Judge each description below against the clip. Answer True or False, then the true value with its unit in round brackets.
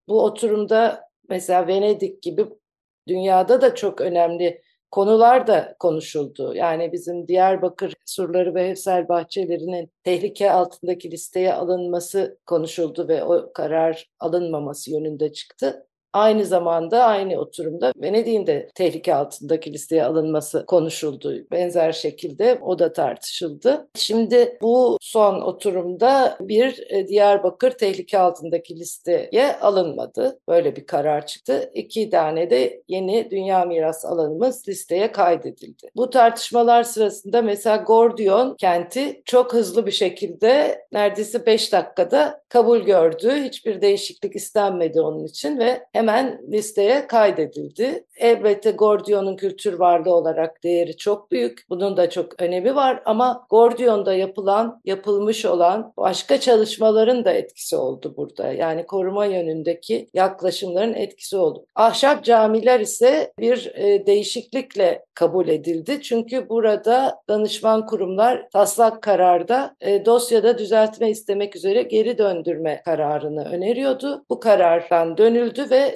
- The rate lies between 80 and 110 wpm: False (120 wpm)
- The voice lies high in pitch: True (200 Hz)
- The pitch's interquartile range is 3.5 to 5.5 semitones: True (5.2 semitones)